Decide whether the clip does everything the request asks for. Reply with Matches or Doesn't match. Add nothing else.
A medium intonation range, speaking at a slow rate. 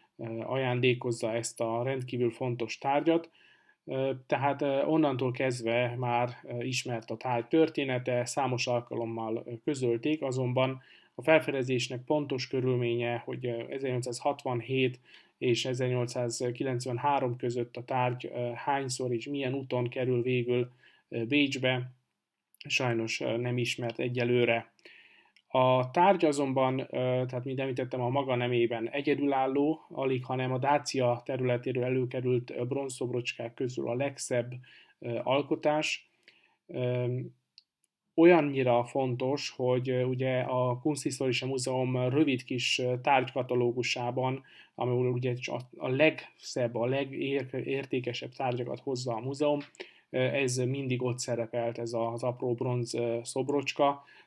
Doesn't match